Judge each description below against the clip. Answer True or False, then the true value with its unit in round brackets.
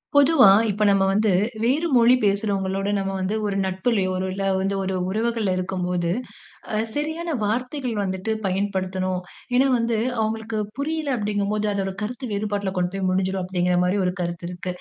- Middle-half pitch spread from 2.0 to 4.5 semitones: True (3.4 semitones)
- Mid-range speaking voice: False (200 Hz)